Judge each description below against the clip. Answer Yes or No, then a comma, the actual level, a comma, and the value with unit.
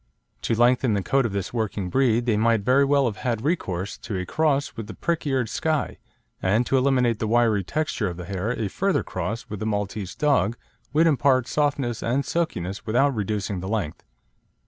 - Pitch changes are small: No, average, 5.0 semitones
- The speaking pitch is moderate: No, low, 115 Hz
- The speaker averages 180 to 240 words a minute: Yes, average, 195 wpm